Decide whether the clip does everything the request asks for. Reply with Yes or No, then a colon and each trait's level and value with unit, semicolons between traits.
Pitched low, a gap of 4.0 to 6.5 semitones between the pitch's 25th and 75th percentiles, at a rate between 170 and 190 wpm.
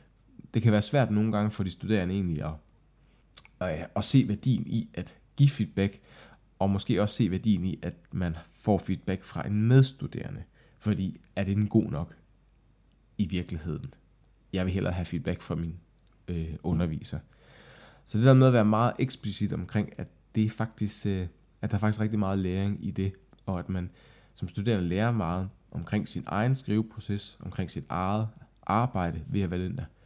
No: low, 100 Hz; average, 3.3 semitones; average, 180 wpm